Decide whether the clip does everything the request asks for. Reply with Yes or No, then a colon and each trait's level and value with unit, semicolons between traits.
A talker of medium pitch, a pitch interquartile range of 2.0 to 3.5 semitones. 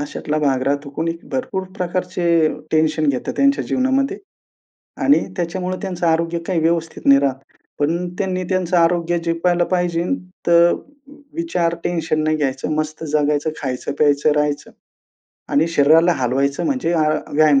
Yes: medium, 165 Hz; average, 3.1 semitones